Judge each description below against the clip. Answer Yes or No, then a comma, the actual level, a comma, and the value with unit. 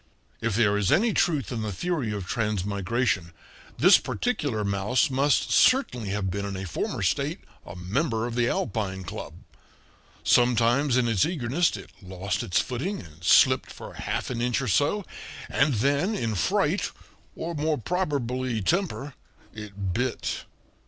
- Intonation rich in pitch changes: Yes, wide, 6.1 semitones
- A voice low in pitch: Yes, low, 120 Hz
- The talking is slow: No, average, 150 wpm